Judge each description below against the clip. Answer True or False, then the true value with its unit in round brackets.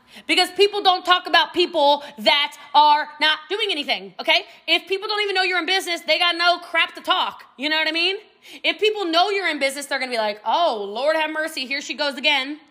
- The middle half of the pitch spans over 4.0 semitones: False (3.5 semitones)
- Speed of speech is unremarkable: False (230 wpm)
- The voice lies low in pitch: False (320 Hz)